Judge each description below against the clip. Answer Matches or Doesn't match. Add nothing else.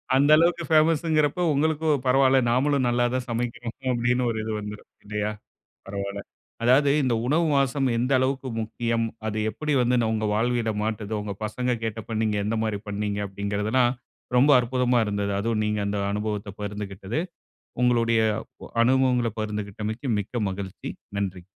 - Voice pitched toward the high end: Doesn't match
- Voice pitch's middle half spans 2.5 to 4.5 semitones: Matches